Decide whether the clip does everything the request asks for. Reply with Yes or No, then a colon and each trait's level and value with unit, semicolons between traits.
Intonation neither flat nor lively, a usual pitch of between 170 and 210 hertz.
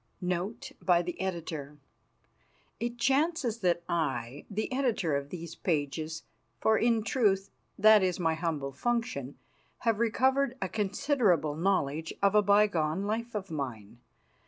No: wide, 6.1 semitones; high, 190 Hz